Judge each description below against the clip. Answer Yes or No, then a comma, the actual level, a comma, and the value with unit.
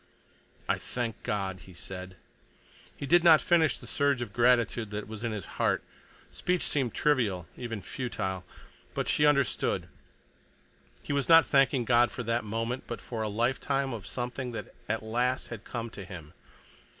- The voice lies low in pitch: Yes, low, 120 Hz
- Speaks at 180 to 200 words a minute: No, average, 165 wpm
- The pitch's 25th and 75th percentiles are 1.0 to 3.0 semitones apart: No, average, 3.9 semitones